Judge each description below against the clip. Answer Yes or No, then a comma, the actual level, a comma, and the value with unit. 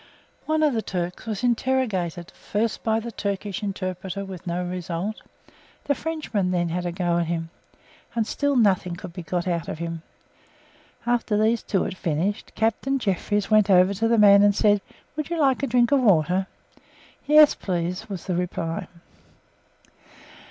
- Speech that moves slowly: No, average, 165 wpm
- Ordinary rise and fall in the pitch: Yes, average, 4.3 semitones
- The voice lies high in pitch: Yes, high, 200 Hz